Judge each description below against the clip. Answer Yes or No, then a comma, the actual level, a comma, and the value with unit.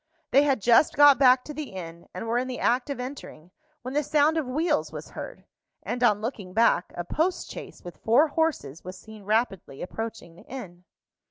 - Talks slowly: No, average, 200 wpm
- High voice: Yes, high, 245 Hz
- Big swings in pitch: Yes, wide, 7.0 semitones